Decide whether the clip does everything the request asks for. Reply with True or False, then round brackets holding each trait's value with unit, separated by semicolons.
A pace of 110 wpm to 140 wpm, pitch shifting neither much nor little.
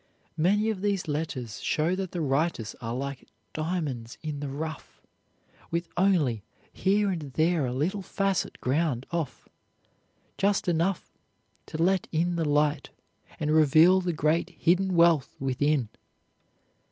True (135 wpm; 3.9 semitones)